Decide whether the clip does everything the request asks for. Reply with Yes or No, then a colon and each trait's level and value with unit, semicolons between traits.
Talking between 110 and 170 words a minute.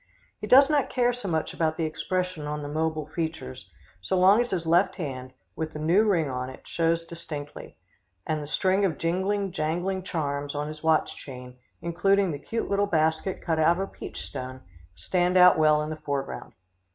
No: average, 195 wpm